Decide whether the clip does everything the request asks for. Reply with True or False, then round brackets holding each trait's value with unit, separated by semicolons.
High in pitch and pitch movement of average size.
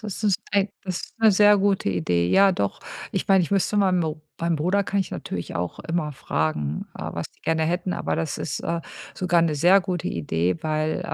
False (170 Hz; 5.0 semitones)